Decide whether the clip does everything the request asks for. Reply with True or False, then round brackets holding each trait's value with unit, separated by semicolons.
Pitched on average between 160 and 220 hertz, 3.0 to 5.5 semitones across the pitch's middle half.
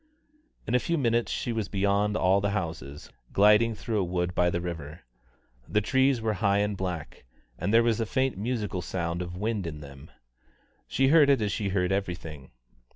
False (100 Hz; 4.4 semitones)